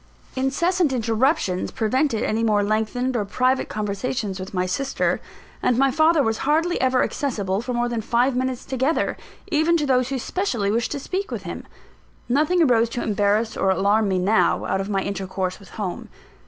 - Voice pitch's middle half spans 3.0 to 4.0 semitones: No, average, 4.7 semitones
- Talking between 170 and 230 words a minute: Yes, average, 180 wpm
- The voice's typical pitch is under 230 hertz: No, high, 240 Hz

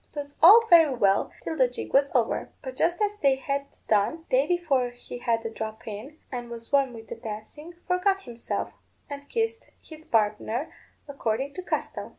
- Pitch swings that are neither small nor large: No, wide, 6.0 semitones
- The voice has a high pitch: Yes, very high, 275 Hz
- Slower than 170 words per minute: No, average, 180 wpm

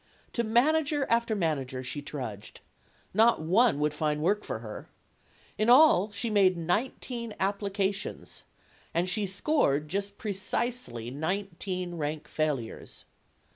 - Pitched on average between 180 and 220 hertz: Yes, high, 190 Hz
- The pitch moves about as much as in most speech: No, wide, 6.5 semitones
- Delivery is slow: Yes, slow, 120 wpm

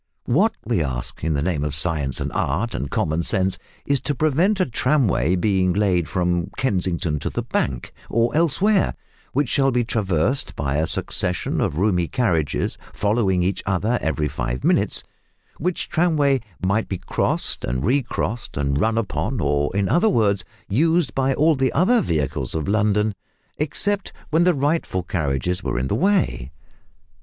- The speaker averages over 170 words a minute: No, average, 165 wpm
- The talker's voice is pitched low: Yes, low, 100 Hz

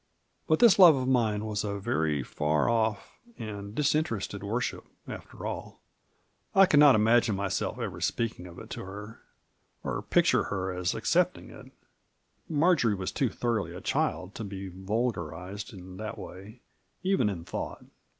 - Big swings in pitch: No, average, 4.2 semitones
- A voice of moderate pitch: No, low, 105 Hz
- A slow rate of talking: No, average, 160 wpm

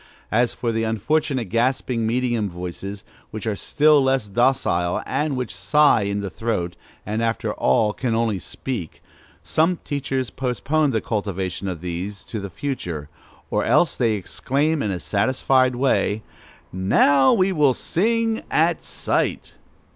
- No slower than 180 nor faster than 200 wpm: No, average, 145 wpm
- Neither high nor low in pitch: No, low, 115 Hz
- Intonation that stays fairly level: No, average, 5.3 semitones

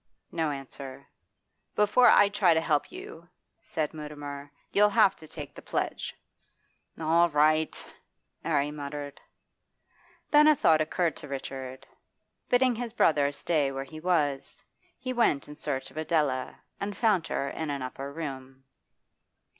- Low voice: No, medium, 155 Hz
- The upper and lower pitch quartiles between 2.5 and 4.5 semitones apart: Yes, average, 3.4 semitones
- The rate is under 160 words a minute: Yes, average, 140 wpm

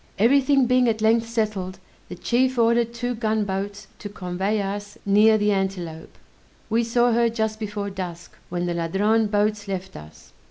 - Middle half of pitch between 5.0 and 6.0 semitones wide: No, average, 3.0 semitones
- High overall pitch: Yes, high, 210 Hz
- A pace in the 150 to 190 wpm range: Yes, average, 165 wpm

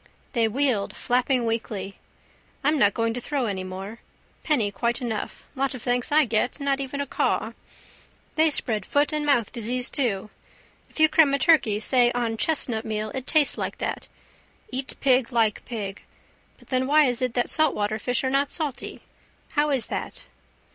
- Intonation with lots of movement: No, average, 3.9 semitones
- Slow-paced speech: No, average, 175 wpm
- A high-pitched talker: Yes, high, 245 Hz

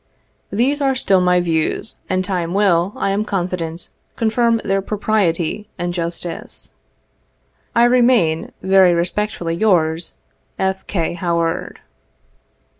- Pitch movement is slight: No, average, 3.7 semitones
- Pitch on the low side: No, medium, 185 Hz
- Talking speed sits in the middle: No, slow, 120 wpm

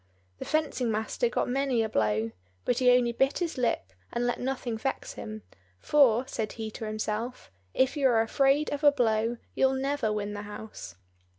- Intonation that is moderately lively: Yes, average, 3.7 semitones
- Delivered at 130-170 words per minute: No, average, 185 wpm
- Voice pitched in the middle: No, high, 240 Hz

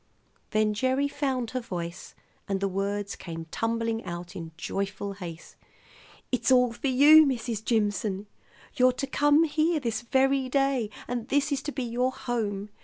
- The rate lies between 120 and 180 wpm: Yes, average, 160 wpm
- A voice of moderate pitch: No, high, 235 Hz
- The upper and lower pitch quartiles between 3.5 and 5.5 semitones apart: Yes, average, 4.9 semitones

